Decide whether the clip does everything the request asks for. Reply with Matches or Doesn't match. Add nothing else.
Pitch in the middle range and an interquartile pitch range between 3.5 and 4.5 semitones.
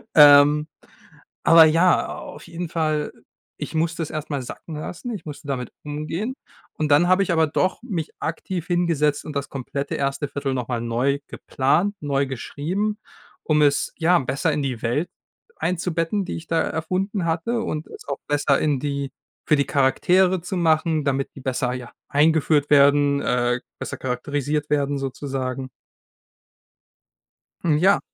Doesn't match